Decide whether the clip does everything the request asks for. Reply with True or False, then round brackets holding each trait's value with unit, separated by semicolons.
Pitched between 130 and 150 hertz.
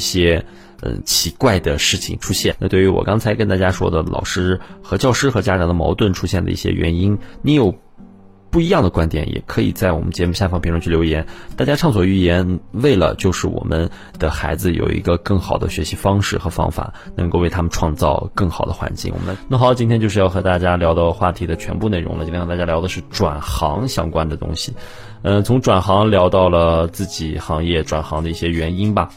False (90 Hz)